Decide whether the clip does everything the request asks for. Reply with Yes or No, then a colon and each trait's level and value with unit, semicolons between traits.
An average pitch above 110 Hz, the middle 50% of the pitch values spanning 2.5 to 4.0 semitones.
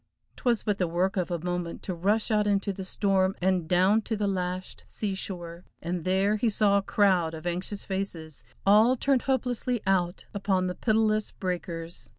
Yes: high, 190 Hz; average, 2.8 semitones